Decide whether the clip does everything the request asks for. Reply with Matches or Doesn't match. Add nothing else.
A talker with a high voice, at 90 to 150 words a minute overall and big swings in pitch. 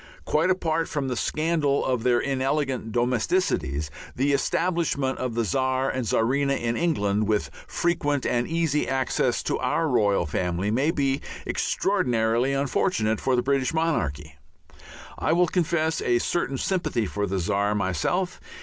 Doesn't match